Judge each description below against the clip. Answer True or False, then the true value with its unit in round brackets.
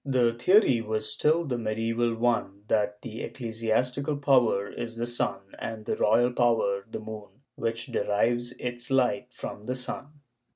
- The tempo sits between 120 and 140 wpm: False (160 wpm)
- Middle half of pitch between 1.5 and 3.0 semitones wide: True (2.5 semitones)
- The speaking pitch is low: True (115 Hz)